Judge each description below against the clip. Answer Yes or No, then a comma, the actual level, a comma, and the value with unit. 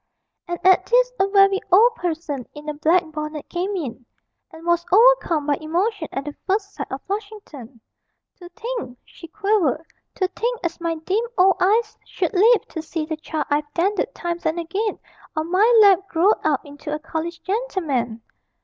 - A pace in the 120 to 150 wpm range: No, average, 175 wpm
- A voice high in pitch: Yes, very high, 345 Hz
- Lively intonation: No, average, 4.6 semitones